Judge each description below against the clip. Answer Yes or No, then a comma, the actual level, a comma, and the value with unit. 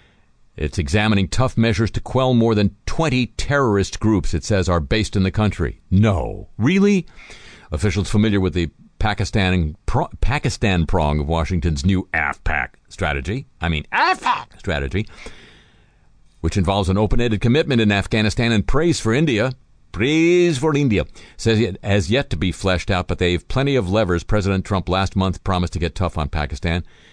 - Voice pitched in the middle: No, low, 100 Hz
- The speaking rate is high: No, average, 165 wpm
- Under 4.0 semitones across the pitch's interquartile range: No, average, 4.3 semitones